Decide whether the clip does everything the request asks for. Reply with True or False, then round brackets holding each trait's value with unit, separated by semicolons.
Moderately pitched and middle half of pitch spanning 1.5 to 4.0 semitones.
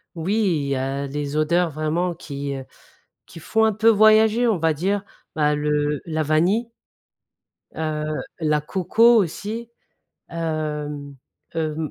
False (160 Hz; 5.2 semitones)